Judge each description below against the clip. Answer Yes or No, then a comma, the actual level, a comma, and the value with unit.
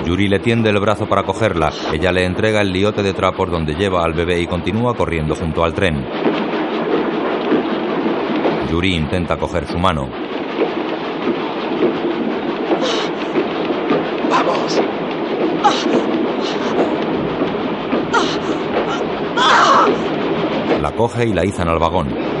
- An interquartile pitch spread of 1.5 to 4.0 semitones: Yes, average, 3.7 semitones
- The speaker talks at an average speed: No, slow, 100 wpm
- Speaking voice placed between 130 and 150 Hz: No, very low, 90 Hz